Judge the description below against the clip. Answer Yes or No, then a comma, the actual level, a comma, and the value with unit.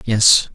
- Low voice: Yes, low, 110 Hz